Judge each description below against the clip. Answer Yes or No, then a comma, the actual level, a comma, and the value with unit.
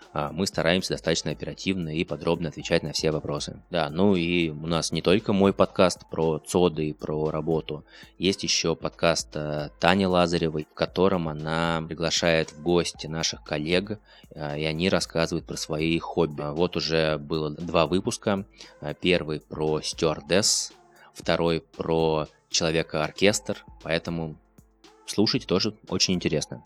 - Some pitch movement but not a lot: No, narrow, 2.3 semitones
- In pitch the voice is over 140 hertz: No, very low, 80 Hz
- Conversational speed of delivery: Yes, average, 135 wpm